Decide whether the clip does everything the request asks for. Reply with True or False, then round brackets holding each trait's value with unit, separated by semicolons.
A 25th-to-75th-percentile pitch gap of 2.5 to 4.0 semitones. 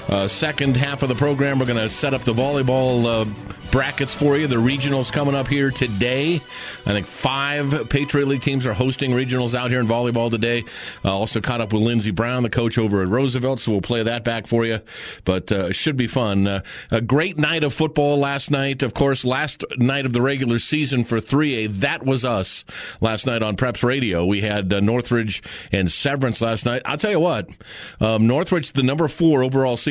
True (3.5 semitones)